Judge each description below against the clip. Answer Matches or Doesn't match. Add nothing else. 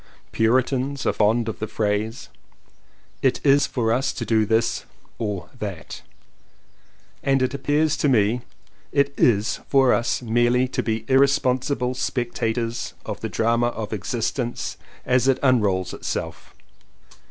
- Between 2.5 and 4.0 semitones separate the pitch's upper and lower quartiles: Matches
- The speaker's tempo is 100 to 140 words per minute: Matches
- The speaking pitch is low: Matches